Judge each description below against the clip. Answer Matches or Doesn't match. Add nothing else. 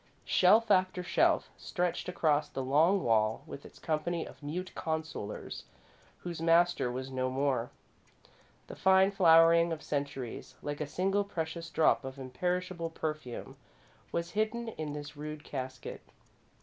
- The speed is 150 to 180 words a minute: Doesn't match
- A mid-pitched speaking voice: Matches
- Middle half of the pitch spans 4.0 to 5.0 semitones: Matches